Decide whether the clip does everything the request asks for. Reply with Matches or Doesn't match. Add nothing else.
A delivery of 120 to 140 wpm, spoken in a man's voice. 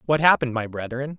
Doesn't match